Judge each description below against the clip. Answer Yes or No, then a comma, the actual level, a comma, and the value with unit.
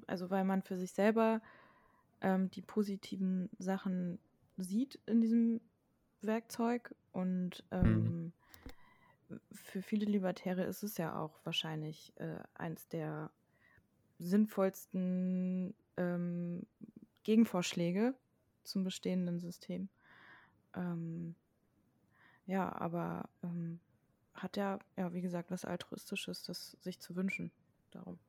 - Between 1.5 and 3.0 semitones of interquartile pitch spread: Yes, narrow, 2.5 semitones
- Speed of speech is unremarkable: No, slow, 105 wpm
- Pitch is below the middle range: No, medium, 185 Hz